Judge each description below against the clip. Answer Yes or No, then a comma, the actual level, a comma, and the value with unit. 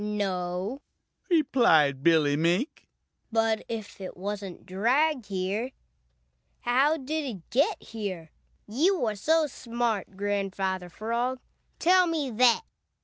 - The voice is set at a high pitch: Yes, high, 220 Hz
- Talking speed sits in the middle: No, slow, 110 wpm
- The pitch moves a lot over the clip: Yes, wide, 5.9 semitones